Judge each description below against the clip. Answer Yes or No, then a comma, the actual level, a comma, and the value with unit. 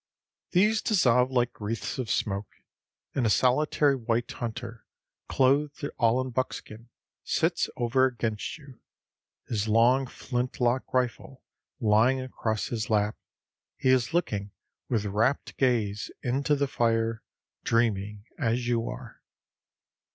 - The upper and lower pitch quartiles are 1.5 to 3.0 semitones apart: Yes, narrow, 2.6 semitones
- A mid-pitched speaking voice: No, low, 120 Hz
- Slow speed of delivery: Yes, slow, 120 wpm